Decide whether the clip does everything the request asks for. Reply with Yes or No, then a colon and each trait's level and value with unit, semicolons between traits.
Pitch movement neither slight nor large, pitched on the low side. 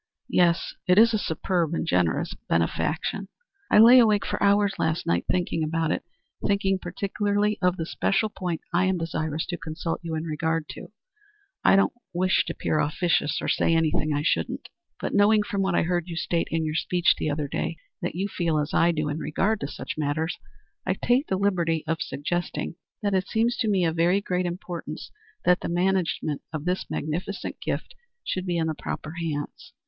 No: average, 3.3 semitones; medium, 175 Hz